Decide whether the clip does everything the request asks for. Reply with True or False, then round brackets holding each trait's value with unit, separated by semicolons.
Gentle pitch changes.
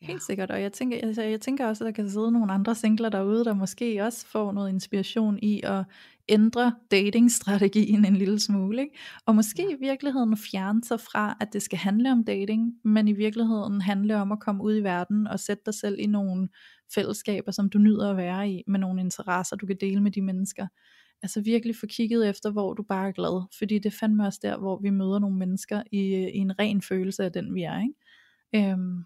True (2.0 semitones)